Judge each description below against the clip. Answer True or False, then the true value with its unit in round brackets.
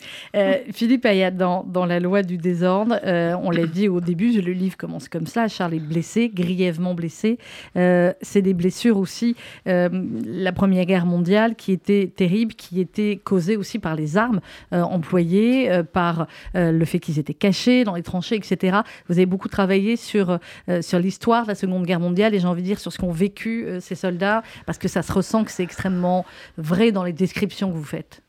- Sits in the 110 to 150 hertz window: False (185 Hz)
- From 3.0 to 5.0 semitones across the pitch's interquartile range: False (2.6 semitones)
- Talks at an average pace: True (210 wpm)